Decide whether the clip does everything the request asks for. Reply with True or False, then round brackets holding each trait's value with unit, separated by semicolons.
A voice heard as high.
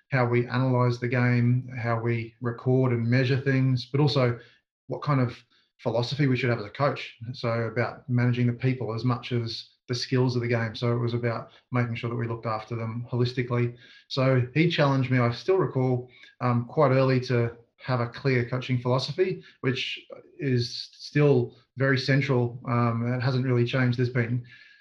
False (125 Hz)